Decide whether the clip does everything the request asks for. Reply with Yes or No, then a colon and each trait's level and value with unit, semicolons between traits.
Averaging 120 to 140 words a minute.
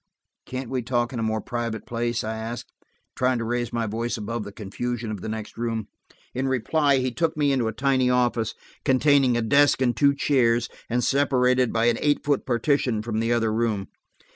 No: average, 200 wpm